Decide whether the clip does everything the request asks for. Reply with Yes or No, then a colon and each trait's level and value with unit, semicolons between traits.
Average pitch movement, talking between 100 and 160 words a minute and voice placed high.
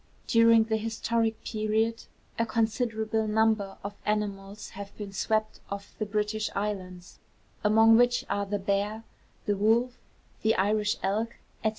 No: narrow, 1.6 semitones; slow, 135 wpm; high, 215 Hz